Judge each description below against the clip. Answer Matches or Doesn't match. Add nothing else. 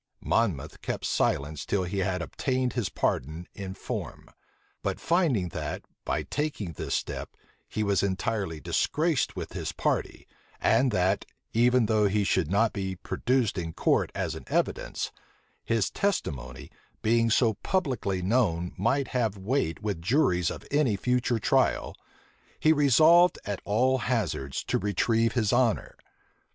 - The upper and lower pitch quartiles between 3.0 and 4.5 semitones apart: Doesn't match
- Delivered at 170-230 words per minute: Doesn't match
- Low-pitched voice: Matches